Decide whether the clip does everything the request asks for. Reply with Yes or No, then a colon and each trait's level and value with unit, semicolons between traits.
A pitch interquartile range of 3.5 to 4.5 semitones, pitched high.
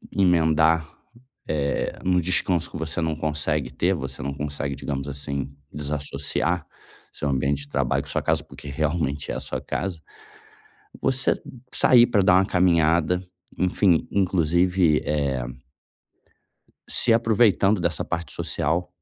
No: average, 3.9 semitones; very low, 80 Hz